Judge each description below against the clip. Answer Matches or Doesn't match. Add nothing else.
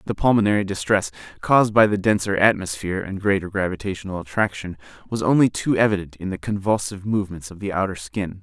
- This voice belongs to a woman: Doesn't match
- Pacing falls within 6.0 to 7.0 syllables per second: Matches